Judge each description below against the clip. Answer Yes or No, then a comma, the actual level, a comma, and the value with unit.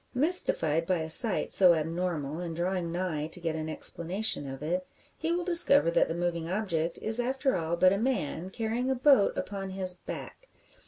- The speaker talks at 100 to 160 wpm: No, average, 190 wpm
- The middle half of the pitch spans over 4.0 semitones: Yes, average, 5.2 semitones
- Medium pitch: Yes, medium, 180 Hz